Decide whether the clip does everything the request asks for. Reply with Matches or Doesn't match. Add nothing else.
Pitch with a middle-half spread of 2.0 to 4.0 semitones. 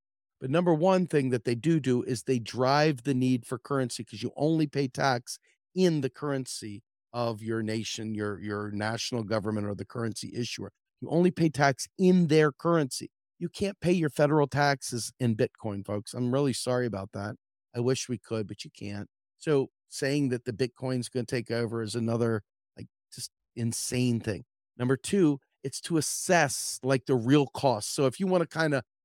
Doesn't match